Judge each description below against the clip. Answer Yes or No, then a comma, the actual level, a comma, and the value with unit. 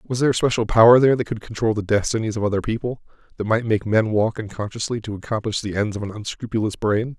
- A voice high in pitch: No, low, 110 Hz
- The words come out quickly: Yes, fast, 235 wpm